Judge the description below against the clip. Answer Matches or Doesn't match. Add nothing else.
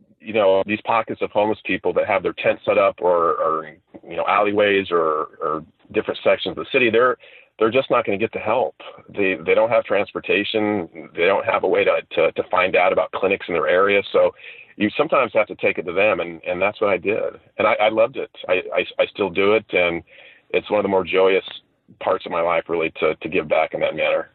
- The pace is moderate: Doesn't match